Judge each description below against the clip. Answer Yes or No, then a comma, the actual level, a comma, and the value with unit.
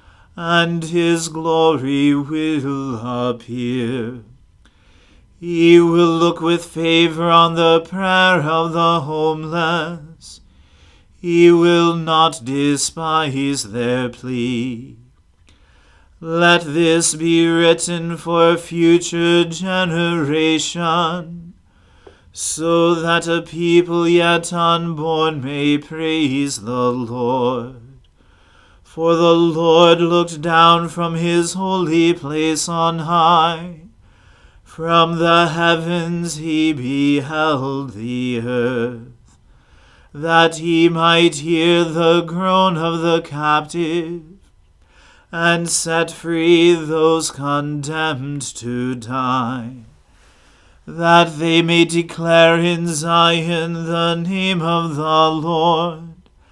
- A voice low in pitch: No, medium, 165 Hz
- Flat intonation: No, average, 3.6 semitones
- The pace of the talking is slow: Yes, slow, 90 wpm